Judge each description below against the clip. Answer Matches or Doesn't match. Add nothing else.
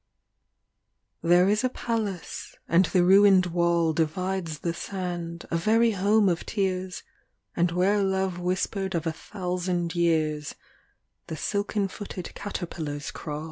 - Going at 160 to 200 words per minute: Doesn't match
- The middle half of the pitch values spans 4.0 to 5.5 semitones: Doesn't match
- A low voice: Doesn't match